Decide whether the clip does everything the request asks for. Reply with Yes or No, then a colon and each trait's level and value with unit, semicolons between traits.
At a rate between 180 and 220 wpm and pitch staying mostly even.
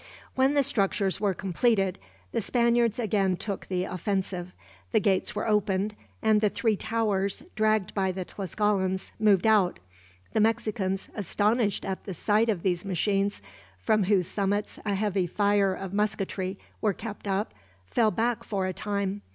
No: average, 155 wpm; narrow, 2.1 semitones